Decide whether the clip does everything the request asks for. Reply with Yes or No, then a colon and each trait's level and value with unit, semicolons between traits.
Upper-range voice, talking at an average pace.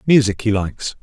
No: low, 110 Hz; average, 175 wpm